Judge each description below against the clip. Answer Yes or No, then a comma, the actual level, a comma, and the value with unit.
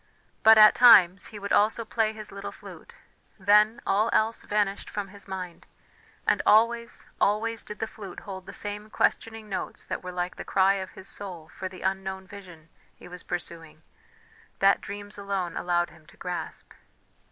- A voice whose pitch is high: Yes, high, 200 Hz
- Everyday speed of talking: Yes, average, 175 wpm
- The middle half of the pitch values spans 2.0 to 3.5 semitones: Yes, narrow, 2.5 semitones